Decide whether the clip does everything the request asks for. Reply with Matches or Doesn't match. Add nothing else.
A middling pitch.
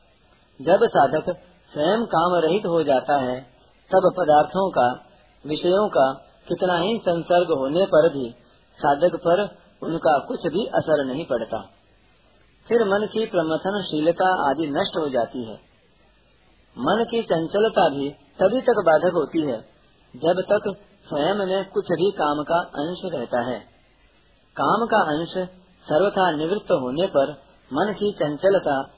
Matches